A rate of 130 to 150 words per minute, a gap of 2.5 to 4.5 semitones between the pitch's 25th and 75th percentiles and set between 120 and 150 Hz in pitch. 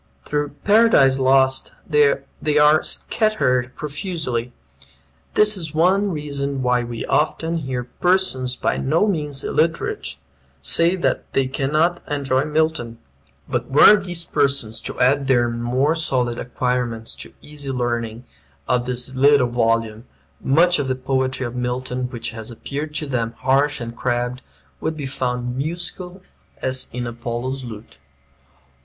Yes: slow, 135 wpm; average, 3.8 semitones; low, 135 Hz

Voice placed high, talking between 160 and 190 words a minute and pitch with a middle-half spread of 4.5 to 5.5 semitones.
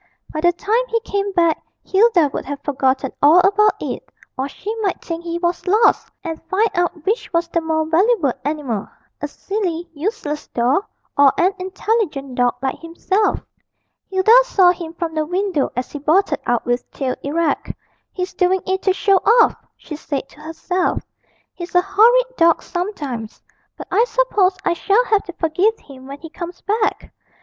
Yes: very high, 345 Hz; average, 175 wpm; average, 4.9 semitones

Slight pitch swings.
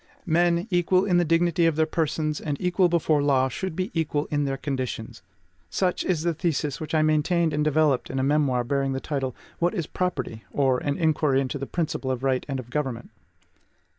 No: average, 3.9 semitones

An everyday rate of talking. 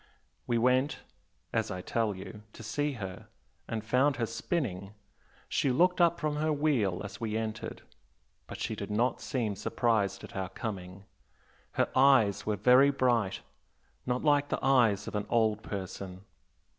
Yes: average, 155 wpm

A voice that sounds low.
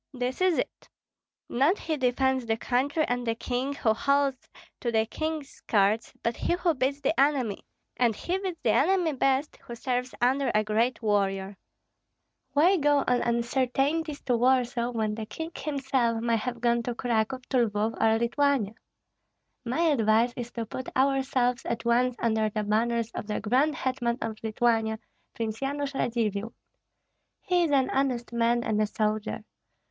No: high, 245 Hz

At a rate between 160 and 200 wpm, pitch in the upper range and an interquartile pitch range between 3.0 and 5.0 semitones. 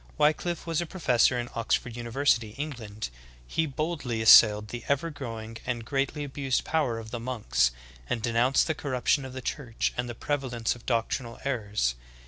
No: average, 170 wpm; low, 125 Hz; average, 3.7 semitones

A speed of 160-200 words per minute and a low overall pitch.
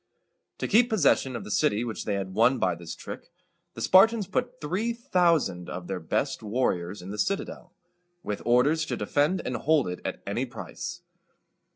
Yes: average, 180 wpm; low, 130 Hz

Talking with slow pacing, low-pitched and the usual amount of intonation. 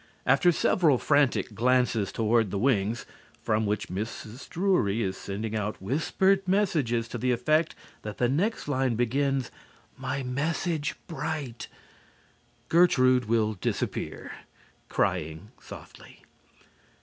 No: slow, 115 wpm; low, 125 Hz; wide, 5.7 semitones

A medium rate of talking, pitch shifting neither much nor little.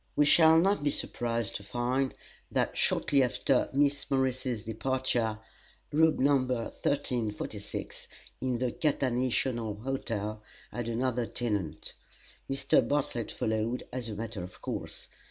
No: slow, 120 wpm; average, 3.0 semitones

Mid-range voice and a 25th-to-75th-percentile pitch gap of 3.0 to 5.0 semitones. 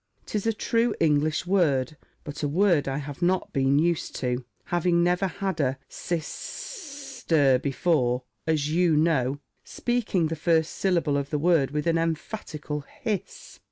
Yes: medium, 160 Hz; average, 3.9 semitones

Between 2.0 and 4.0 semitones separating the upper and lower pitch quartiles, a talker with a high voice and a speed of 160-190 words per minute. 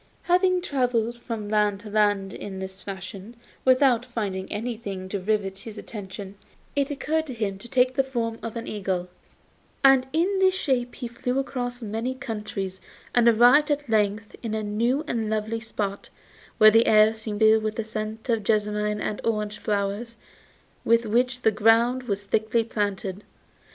Yes: average, 3.0 semitones; high, 220 Hz; average, 165 wpm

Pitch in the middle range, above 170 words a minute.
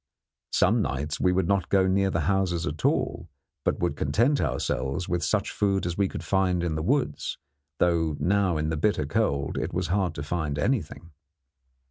No: very low, 85 Hz; average, 185 wpm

